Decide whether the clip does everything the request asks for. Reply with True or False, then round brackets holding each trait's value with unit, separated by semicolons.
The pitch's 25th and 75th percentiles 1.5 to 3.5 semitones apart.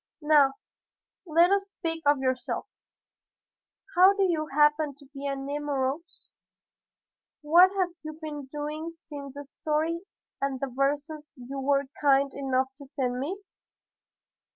True (2.6 semitones)